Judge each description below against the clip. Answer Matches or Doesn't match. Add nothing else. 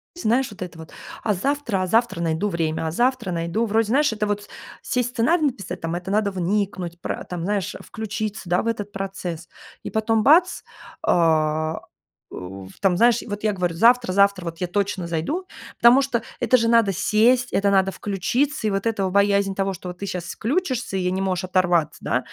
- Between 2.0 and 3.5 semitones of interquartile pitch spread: Doesn't match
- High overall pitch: Matches